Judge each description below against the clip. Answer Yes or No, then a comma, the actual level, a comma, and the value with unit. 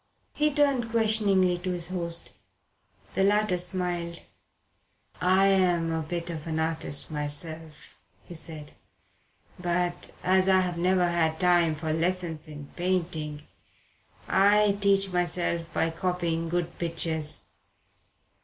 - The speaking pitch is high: No, medium, 175 Hz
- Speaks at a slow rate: Yes, slow, 115 wpm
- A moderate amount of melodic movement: No, narrow, 2.3 semitones